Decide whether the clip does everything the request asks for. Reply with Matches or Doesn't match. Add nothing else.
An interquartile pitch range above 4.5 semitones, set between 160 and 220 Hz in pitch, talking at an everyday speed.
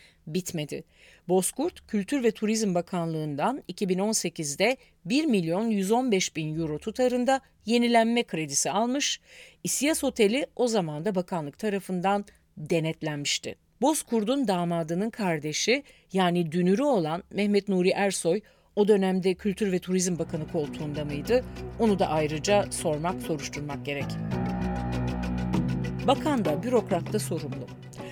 Matches